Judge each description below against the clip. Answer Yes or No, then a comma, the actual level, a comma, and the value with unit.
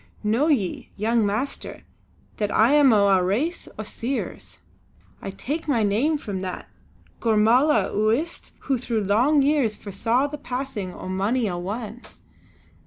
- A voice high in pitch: Yes, high, 225 Hz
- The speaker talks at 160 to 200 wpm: No, average, 150 wpm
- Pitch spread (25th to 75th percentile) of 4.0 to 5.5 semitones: Yes, average, 5.1 semitones